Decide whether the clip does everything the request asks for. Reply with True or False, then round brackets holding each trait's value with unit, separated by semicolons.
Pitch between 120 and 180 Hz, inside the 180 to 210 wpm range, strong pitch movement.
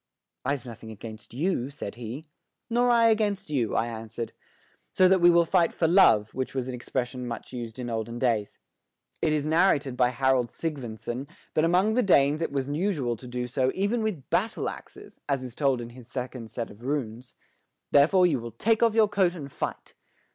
True (135 Hz; 195 wpm; 6.3 semitones)